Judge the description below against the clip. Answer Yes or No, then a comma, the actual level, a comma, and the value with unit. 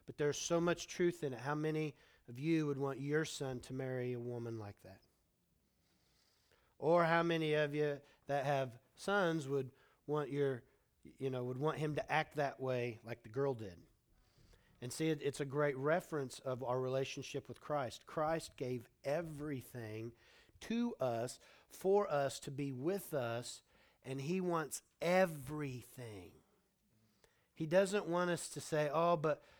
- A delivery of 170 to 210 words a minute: No, average, 160 wpm